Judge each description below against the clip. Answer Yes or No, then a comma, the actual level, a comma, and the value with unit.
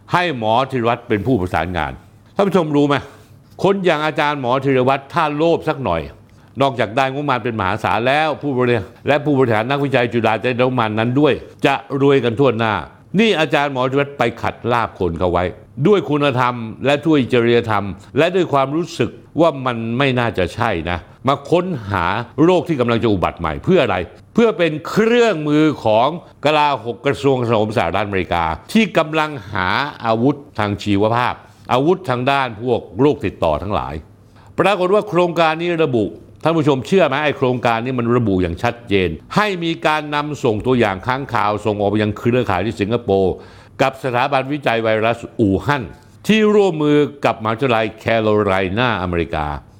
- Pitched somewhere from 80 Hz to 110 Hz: No, low, 125 Hz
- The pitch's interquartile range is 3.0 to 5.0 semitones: No, wide, 5.4 semitones